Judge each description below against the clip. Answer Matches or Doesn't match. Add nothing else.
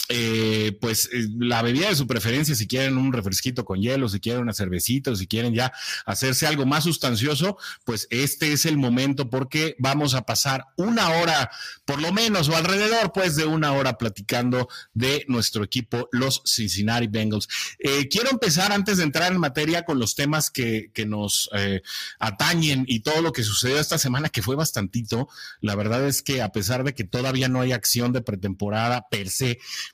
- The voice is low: Matches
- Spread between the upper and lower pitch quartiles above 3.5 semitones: Matches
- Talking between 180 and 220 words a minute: Matches